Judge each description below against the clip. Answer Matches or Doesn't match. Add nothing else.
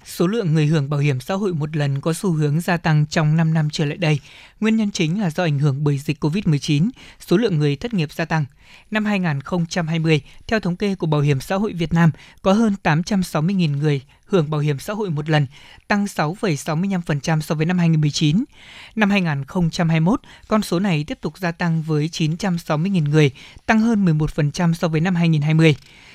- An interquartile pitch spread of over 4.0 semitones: Doesn't match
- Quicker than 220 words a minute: Doesn't match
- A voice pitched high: Doesn't match